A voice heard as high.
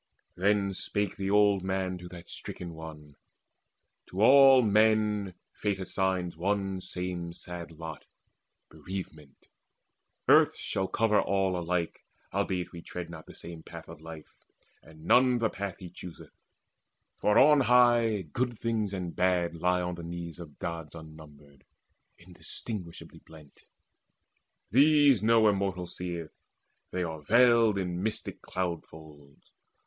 No: very low, 90 Hz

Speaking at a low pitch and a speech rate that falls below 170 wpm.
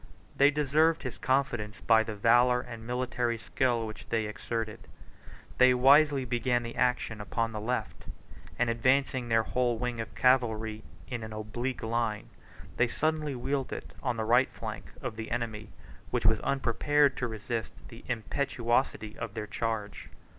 Yes: low, 120 Hz; average, 160 wpm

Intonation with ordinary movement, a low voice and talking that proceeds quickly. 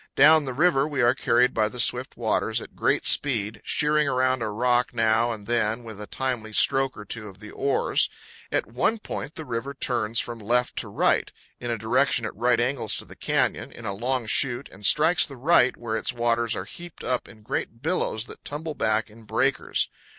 Yes: average, 3.3 semitones; low, 120 Hz; fast, 210 wpm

